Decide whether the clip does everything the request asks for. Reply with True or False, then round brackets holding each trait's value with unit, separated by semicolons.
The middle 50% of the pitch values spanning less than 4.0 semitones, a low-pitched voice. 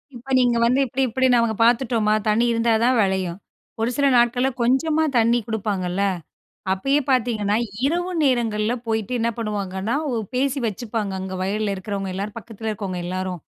False (3.5 semitones; 225 Hz)